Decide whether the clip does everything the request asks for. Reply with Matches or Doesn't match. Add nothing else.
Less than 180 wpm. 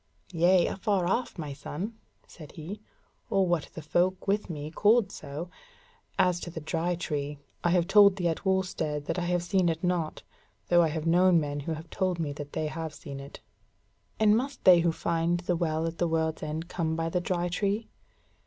Doesn't match